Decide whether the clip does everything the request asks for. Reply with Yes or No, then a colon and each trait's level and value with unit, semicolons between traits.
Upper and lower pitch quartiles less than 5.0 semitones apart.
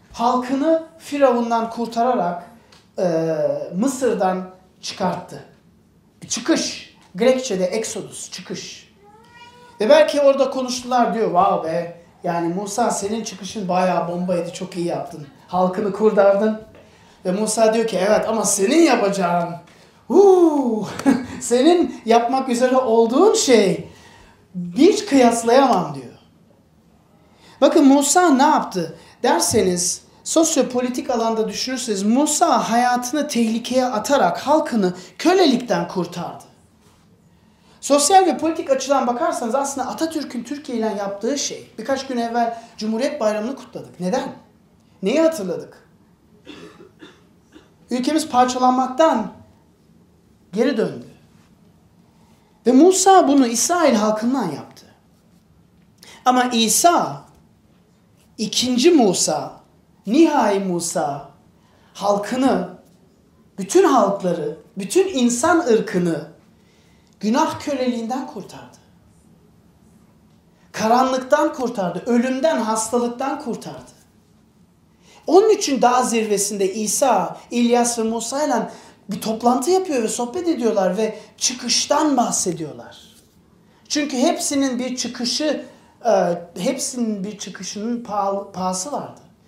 No: wide, 5.5 semitones